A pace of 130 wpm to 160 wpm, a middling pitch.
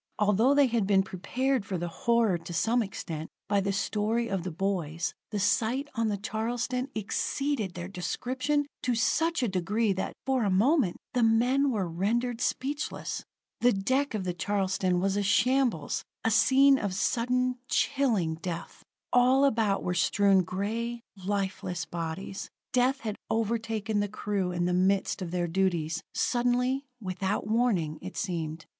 No: average, 155 wpm; high, 210 Hz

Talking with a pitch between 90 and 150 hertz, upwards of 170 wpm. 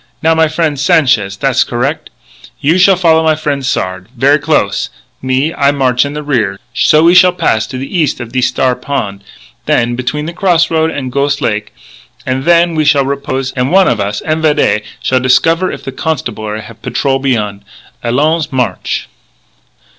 Yes: medium, 140 Hz; average, 180 wpm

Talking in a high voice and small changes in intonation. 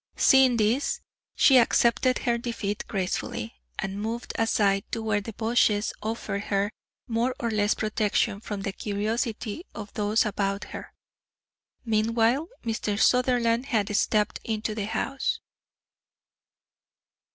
Yes: high, 220 Hz; narrow, 2.3 semitones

